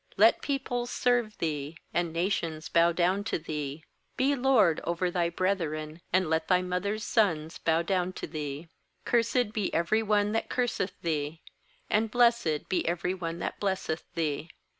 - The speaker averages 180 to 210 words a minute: No, average, 155 wpm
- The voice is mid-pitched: Yes, medium, 180 Hz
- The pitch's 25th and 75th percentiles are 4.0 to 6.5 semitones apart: Yes, average, 4.6 semitones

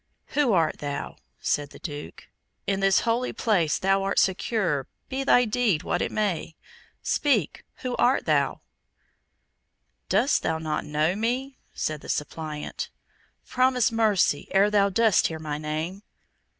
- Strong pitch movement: Yes, wide, 6.7 semitones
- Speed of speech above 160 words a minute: No, average, 140 wpm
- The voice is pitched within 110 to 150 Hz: No, high, 195 Hz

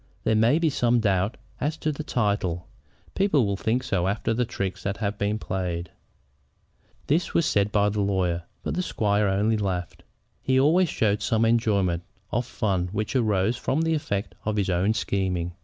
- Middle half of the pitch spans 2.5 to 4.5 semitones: Yes, average, 3.9 semitones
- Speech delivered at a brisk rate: No, average, 185 wpm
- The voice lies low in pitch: Yes, low, 105 Hz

